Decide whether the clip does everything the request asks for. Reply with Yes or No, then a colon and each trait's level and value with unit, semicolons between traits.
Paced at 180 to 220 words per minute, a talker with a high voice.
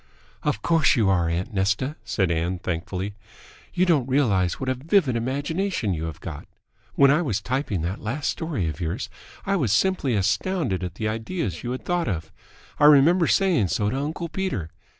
No: average, 185 wpm; low, 120 Hz